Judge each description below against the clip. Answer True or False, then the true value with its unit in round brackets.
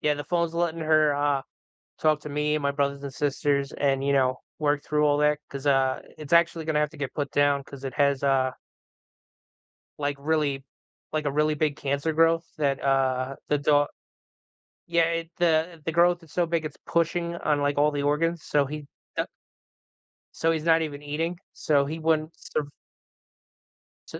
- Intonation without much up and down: True (2.2 semitones)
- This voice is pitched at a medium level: True (150 Hz)